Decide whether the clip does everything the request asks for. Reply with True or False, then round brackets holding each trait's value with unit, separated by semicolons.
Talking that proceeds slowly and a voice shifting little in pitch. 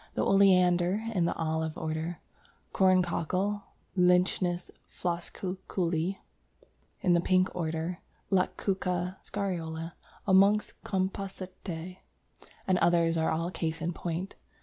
True (100 wpm; 2.1 semitones)